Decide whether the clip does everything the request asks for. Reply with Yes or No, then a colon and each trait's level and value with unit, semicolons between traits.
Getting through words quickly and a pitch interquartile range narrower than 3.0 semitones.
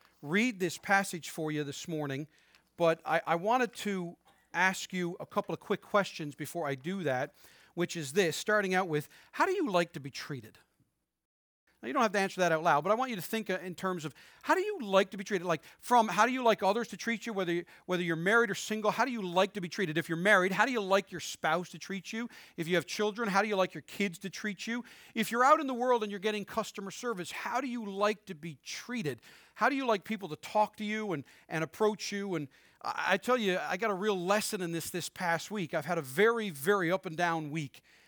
No: fast, 255 wpm; average, 4.3 semitones